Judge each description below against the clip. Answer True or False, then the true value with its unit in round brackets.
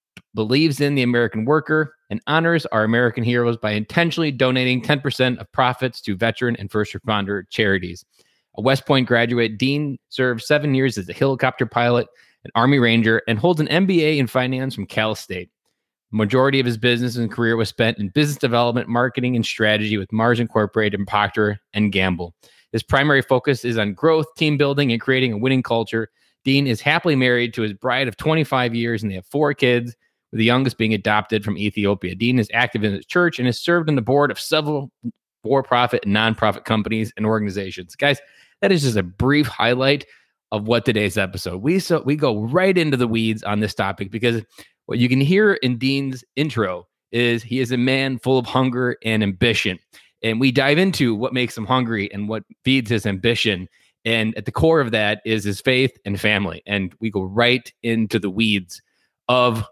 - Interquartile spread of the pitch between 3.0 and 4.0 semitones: True (3.7 semitones)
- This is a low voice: True (120 Hz)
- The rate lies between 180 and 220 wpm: True (195 wpm)